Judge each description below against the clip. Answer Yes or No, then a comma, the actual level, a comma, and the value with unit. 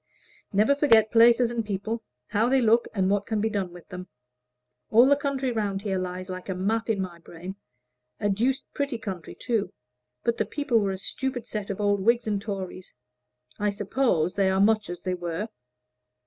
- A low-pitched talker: No, high, 205 Hz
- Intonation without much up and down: No, average, 3.5 semitones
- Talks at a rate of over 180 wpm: Yes, average, 190 wpm